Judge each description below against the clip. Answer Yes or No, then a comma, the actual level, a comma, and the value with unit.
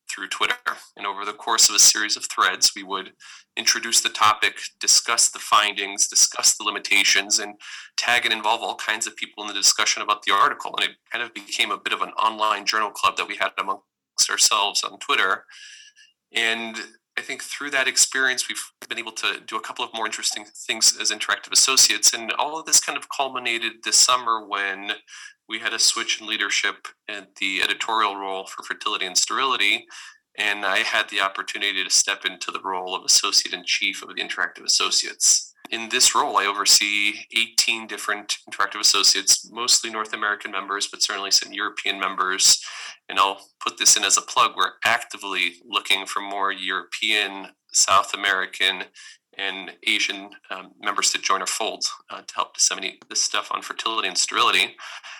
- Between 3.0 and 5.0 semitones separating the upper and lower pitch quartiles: No, narrow, 2.5 semitones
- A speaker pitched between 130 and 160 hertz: No, low, 105 Hz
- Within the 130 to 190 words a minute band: Yes, average, 185 wpm